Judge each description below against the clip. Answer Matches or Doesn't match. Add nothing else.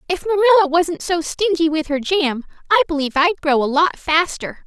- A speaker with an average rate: Matches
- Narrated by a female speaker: Matches